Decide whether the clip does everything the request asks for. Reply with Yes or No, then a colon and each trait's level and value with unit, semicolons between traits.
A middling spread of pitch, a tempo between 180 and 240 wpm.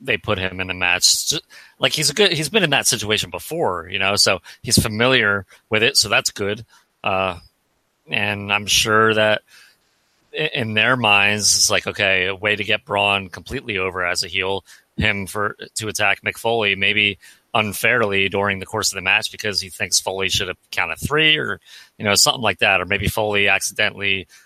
No: narrow, 2.2 semitones; average, 190 wpm